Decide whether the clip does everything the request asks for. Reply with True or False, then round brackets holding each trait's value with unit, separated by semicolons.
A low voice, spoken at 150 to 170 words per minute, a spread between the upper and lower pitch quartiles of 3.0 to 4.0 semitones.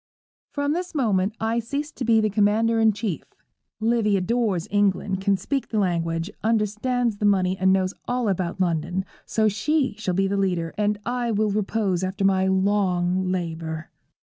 False (205 Hz; 165 wpm; 3.3 semitones)